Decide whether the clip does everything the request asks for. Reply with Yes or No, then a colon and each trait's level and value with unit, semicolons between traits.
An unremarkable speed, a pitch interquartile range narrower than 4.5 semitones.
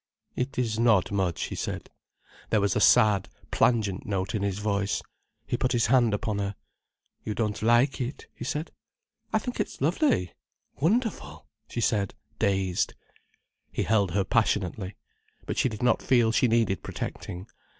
Yes: average, 155 wpm; average, 3.6 semitones